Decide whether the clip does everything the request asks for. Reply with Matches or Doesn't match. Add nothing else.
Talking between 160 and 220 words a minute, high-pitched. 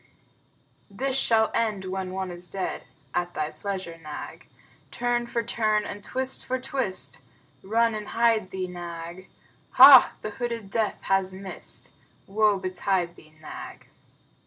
Doesn't match